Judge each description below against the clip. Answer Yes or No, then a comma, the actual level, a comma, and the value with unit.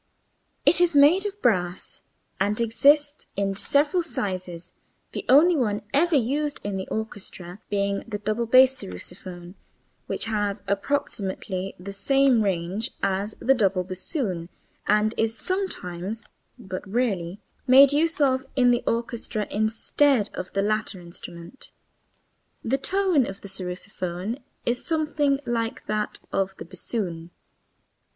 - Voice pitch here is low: No, high, 215 Hz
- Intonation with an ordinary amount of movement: No, wide, 6.0 semitones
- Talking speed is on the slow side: Yes, slow, 130 wpm